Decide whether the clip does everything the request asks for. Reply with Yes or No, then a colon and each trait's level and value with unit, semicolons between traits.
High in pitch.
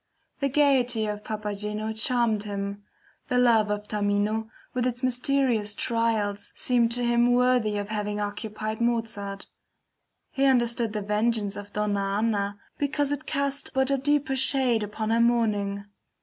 Yes: high, 225 Hz